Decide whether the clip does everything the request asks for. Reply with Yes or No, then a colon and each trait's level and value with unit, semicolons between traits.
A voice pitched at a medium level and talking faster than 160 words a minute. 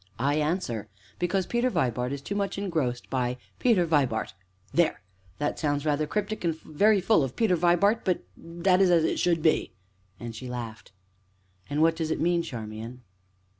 Yes: medium, 160 Hz; average, 170 wpm